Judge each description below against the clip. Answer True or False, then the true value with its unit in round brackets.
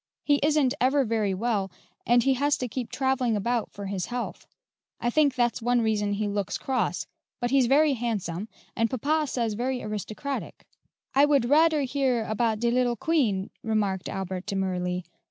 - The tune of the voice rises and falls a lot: False (4.4 semitones)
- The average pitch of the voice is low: False (240 Hz)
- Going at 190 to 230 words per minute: False (170 wpm)